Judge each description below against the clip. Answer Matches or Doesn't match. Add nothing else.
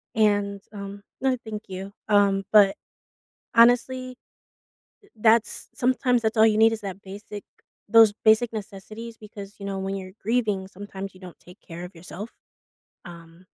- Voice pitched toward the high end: Matches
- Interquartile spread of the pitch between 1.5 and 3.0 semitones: Matches